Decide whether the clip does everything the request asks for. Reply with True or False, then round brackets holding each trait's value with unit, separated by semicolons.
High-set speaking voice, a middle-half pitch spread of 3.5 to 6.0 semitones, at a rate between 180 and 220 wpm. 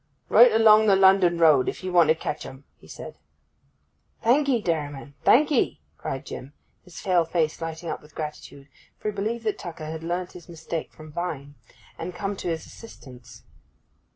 False (170 Hz; 4.3 semitones; 185 wpm)